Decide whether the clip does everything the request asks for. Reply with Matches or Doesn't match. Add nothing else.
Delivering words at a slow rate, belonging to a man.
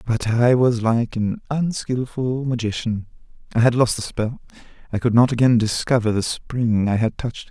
Doesn't match